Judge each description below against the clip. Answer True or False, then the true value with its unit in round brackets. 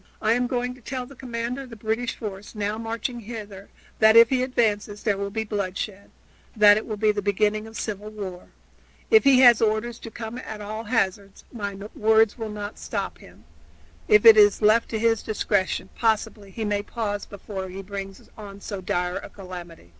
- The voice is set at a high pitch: True (215 Hz)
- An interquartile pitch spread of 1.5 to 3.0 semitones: True (2.4 semitones)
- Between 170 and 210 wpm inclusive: True (195 wpm)